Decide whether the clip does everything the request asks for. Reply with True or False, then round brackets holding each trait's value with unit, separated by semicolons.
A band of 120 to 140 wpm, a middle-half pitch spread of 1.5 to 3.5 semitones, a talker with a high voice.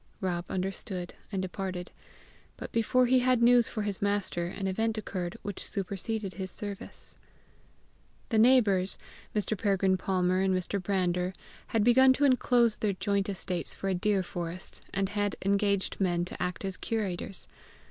False (155 wpm; 2.8 semitones; 195 Hz)